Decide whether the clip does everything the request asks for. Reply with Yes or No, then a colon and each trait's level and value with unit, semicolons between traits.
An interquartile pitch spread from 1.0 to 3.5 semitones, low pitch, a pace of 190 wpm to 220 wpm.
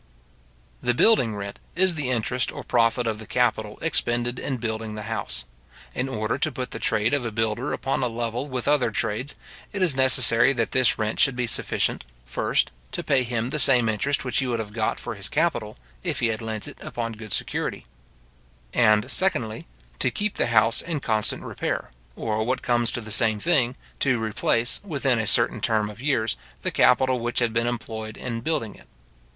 Yes: average, 2.9 semitones; low, 120 Hz; average, 195 wpm